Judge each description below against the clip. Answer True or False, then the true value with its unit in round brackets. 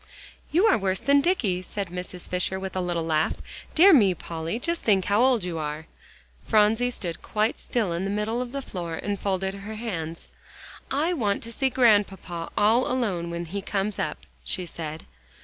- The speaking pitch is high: True (200 Hz)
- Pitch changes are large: False (4.9 semitones)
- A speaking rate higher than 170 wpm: True (185 wpm)